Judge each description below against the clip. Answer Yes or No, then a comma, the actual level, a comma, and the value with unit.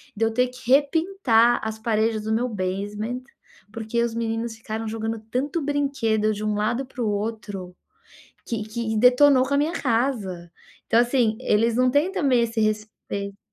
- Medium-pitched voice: No, high, 225 Hz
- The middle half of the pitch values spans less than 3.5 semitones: Yes, average, 2.8 semitones